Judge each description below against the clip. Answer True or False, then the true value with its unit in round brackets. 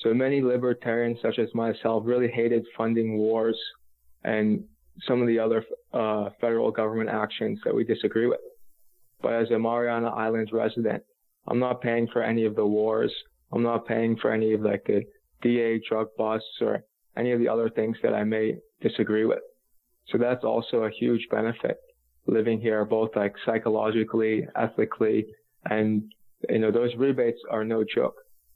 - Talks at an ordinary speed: True (165 wpm)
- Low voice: True (115 Hz)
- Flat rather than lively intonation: True (1.4 semitones)